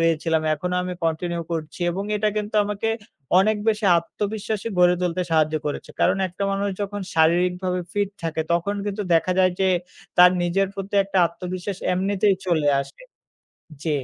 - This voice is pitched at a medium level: Yes, medium, 180 Hz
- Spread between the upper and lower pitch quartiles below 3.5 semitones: Yes, average, 3.1 semitones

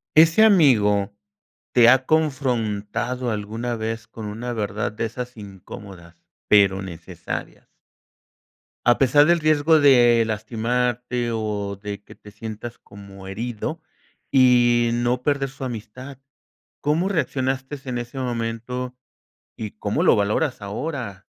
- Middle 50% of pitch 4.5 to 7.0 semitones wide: No, average, 3.8 semitones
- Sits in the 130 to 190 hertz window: No, low, 120 Hz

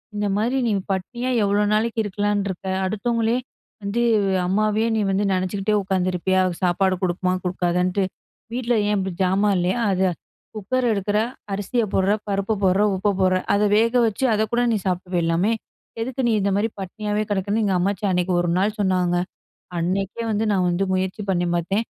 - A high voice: Yes, high, 195 Hz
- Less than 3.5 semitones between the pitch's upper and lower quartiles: Yes, narrow, 2.5 semitones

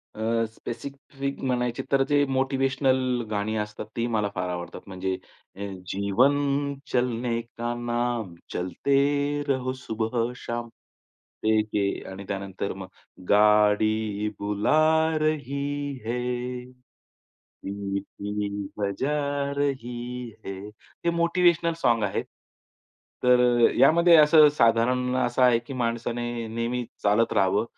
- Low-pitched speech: Yes, low, 120 Hz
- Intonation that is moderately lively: Yes, average, 4.1 semitones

